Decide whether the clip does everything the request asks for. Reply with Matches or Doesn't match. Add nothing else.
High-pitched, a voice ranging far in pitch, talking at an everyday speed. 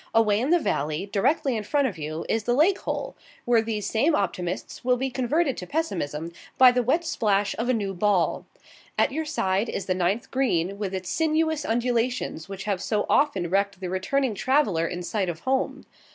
Matches